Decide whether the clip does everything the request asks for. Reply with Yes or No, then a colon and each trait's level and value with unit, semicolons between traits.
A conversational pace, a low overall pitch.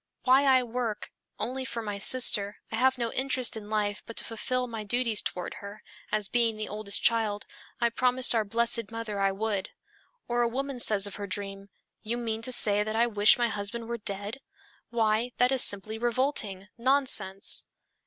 No: average, 185 wpm; high, 225 Hz